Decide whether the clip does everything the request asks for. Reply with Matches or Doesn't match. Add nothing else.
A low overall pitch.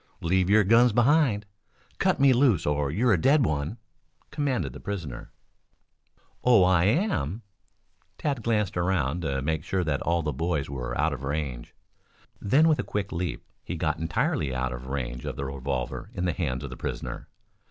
Matches